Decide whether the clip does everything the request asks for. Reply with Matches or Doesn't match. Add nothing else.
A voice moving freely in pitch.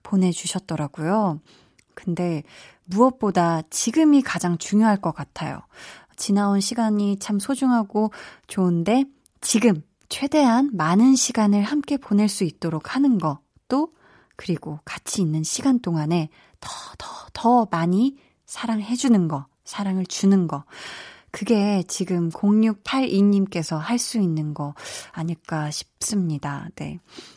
Matches